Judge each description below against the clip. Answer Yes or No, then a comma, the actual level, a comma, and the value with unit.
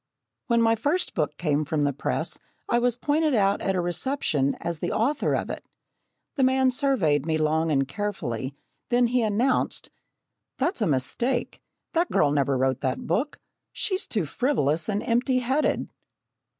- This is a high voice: Yes, high, 205 Hz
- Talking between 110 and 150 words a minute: No, average, 165 wpm